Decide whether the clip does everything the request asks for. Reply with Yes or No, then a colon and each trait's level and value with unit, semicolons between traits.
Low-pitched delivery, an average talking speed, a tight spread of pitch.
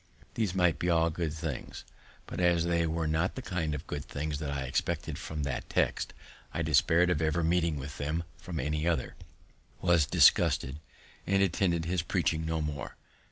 Yes: very low, 80 Hz; average, 180 wpm; narrow, 2.3 semitones